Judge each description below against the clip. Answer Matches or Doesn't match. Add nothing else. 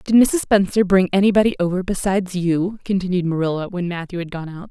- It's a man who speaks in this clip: Doesn't match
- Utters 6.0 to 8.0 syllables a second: Matches